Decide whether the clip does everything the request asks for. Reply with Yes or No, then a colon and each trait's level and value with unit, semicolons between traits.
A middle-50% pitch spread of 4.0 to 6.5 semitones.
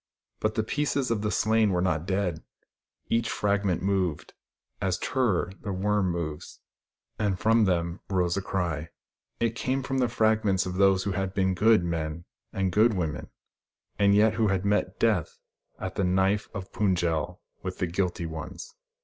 No: average, 3.2 semitones